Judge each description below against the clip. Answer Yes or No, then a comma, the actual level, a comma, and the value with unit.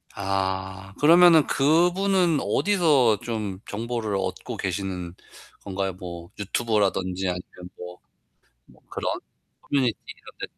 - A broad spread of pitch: Yes, wide, 6.9 semitones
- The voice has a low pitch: Yes, low, 100 Hz